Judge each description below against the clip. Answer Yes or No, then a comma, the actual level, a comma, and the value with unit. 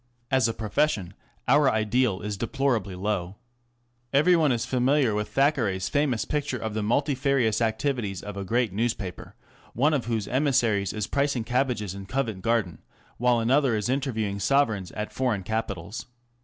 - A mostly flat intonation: No, average, 4.5 semitones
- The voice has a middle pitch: No, low, 115 Hz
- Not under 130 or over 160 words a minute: Yes, average, 155 wpm